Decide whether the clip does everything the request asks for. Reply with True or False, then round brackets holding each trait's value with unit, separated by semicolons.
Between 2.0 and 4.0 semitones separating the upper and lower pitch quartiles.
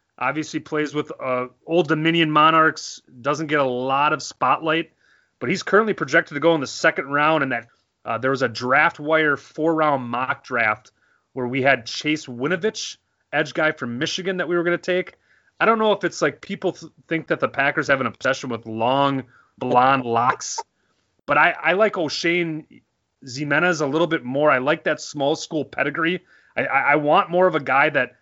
True (3.5 semitones)